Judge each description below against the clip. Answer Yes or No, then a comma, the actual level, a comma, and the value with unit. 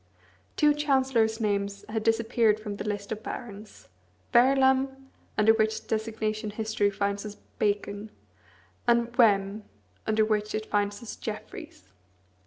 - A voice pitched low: No, high, 215 Hz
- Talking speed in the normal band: No, slow, 125 wpm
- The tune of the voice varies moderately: No, narrow, 2.1 semitones